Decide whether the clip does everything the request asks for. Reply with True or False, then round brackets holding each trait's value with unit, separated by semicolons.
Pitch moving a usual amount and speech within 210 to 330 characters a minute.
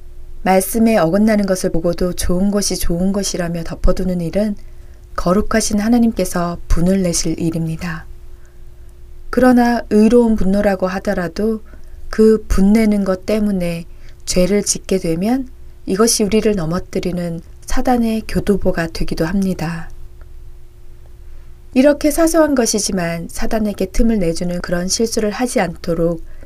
True (4.3 semitones; 285 characters per minute)